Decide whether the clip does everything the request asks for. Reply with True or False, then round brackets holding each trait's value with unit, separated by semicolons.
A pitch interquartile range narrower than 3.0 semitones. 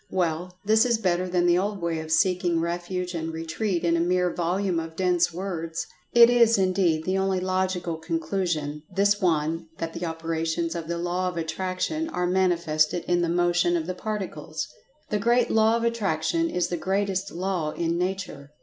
True (2.6 semitones)